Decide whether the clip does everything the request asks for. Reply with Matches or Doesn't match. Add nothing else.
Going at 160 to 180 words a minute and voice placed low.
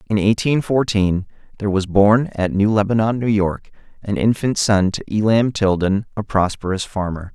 Matches